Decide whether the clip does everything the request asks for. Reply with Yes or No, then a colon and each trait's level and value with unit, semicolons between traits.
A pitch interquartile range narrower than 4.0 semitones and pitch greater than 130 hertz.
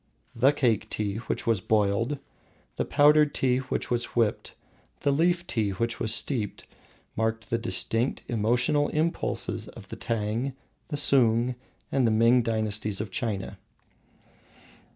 No: average, 3.5 semitones; low, 115 Hz